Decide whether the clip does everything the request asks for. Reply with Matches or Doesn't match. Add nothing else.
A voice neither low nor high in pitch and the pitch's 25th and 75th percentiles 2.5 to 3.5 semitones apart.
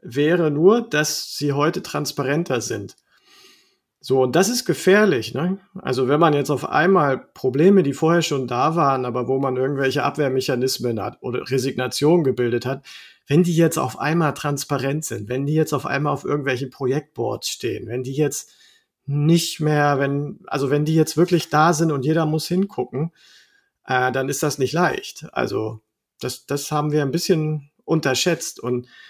Doesn't match